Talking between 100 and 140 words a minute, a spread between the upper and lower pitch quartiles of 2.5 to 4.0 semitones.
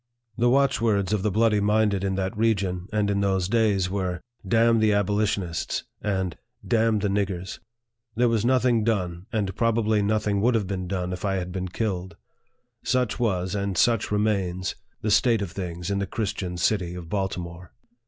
No: average, 185 wpm; average, 3.0 semitones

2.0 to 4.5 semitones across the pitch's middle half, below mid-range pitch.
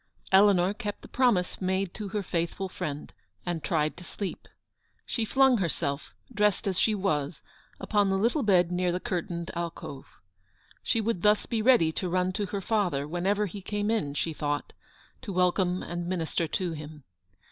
No: average, 3.4 semitones; medium, 185 Hz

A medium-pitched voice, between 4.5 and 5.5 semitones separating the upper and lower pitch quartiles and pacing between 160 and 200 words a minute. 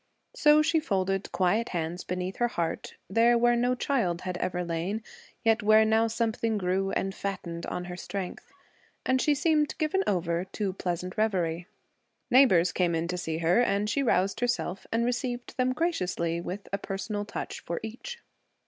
No: high, 200 Hz; average, 5.1 semitones; average, 170 wpm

